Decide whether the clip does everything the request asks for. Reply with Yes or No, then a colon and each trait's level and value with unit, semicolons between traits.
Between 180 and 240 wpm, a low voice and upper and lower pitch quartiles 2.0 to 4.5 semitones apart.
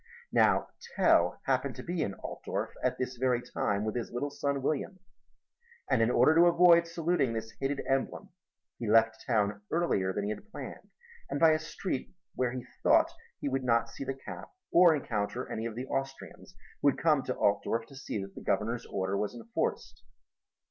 No: average, 190 wpm; low, 130 Hz; average, 5.2 semitones